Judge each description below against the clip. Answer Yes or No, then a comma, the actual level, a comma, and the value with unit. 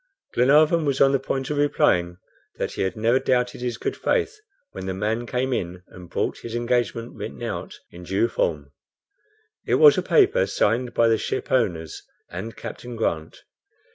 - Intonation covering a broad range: Yes, wide, 6.0 semitones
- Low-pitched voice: Yes, low, 120 Hz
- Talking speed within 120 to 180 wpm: Yes, average, 170 wpm